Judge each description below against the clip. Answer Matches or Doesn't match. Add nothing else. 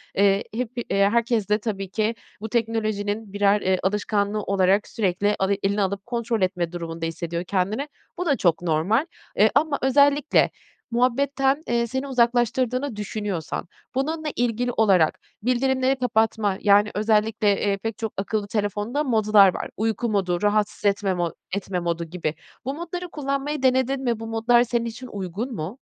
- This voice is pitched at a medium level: Doesn't match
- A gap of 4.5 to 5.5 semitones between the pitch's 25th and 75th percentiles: Doesn't match